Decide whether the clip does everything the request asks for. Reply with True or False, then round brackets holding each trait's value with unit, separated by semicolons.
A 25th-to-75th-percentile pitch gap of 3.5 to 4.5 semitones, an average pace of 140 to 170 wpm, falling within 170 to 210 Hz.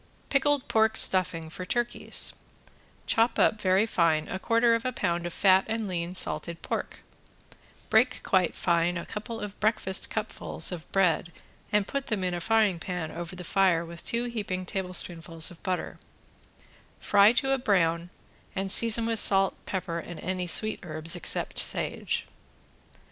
True (4.2 semitones; 160 wpm; 185 Hz)